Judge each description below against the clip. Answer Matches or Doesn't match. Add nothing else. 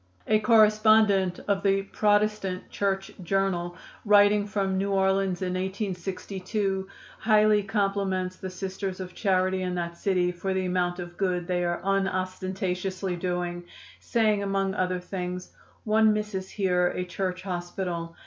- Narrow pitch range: Matches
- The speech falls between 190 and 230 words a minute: Doesn't match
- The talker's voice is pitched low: Doesn't match